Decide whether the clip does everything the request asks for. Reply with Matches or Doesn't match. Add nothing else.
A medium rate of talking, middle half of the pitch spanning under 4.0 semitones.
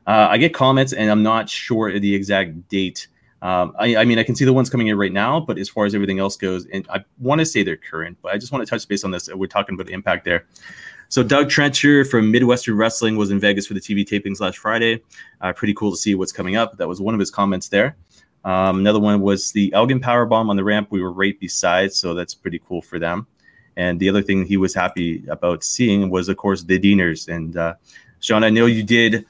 Doesn't match